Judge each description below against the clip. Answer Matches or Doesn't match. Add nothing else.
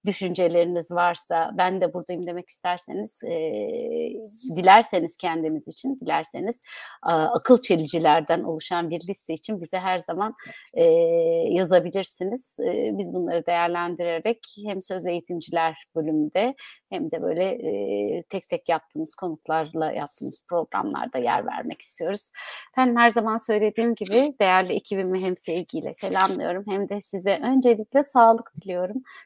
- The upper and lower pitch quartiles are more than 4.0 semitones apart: Matches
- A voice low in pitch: Doesn't match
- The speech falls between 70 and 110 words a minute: Doesn't match